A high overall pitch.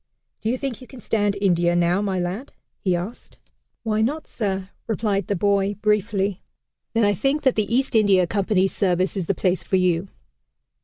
Yes: high, 200 Hz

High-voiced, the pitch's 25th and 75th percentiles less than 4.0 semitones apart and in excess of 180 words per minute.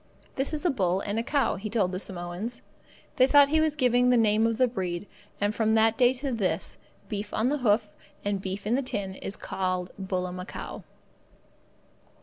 No: high, 215 Hz; average, 4.7 semitones; average, 190 wpm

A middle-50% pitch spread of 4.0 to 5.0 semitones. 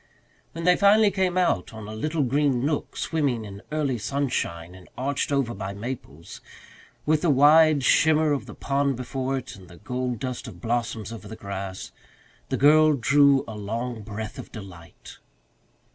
No: wide, 5.4 semitones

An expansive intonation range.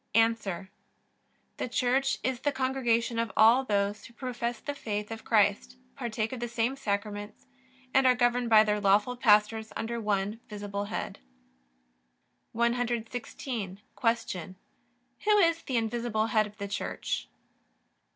No: average, 2.7 semitones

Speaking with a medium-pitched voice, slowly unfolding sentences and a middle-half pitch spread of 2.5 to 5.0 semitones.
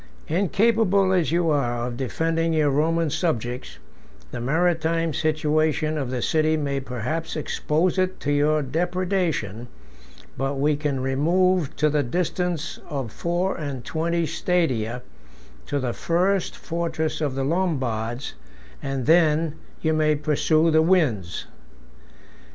Yes: medium, 155 Hz; slow, 125 wpm; average, 3.6 semitones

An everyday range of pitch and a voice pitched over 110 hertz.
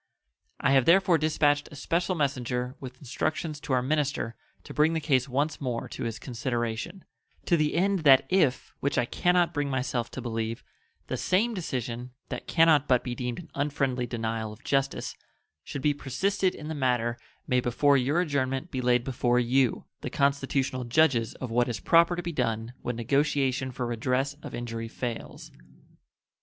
Yes: average, 3.7 semitones; low, 135 Hz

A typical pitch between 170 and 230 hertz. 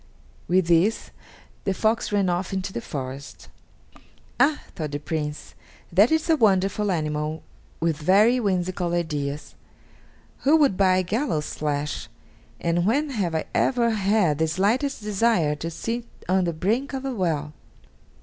Yes: medium, 185 Hz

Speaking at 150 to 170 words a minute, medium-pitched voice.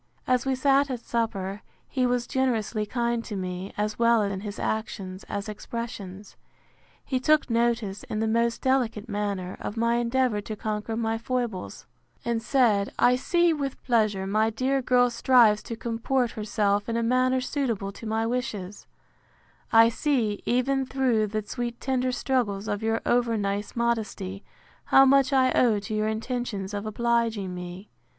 No: average, 160 wpm; high, 230 Hz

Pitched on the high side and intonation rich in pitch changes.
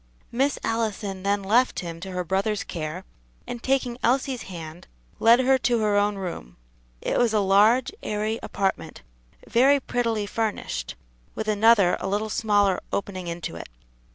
No: high, 210 Hz; average, 3.5 semitones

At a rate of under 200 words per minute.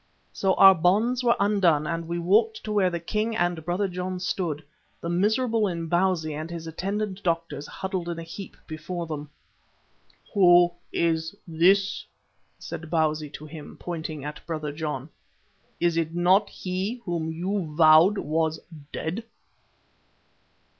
Yes: average, 140 wpm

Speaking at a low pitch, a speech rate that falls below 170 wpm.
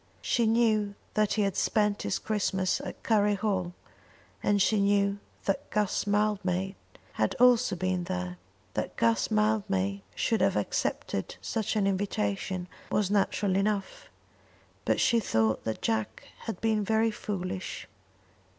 No: high, 200 Hz; slow, 135 wpm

